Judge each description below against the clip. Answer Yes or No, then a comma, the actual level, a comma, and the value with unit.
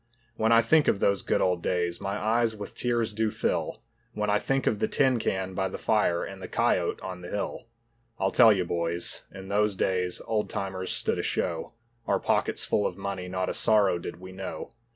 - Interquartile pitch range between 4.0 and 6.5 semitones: No, average, 2.9 semitones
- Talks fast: Yes, fast, 215 wpm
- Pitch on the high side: No, low, 100 Hz